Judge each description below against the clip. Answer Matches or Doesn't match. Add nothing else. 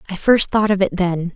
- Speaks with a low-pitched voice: Doesn't match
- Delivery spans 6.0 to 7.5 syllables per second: Doesn't match